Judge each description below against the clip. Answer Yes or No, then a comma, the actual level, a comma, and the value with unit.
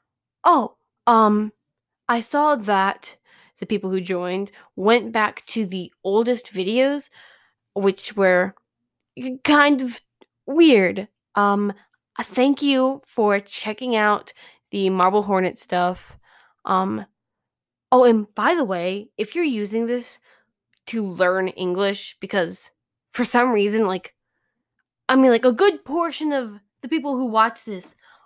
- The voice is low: No, high, 215 Hz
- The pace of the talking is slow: Yes, slow, 125 wpm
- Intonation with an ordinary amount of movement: Yes, average, 4.8 semitones